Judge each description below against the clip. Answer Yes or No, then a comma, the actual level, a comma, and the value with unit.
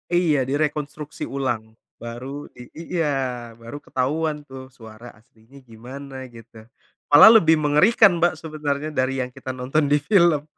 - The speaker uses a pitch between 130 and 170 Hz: Yes, medium, 140 Hz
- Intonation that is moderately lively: Yes, average, 3.4 semitones